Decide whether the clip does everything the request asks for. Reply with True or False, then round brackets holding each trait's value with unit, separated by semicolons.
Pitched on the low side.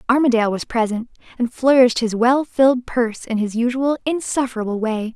False (240 Hz)